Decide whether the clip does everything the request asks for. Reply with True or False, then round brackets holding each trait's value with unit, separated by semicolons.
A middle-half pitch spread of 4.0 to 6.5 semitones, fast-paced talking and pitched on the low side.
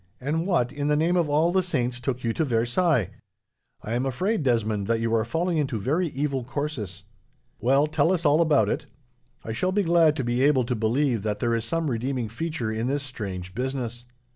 True (5.1 semitones; 210 wpm; 130 Hz)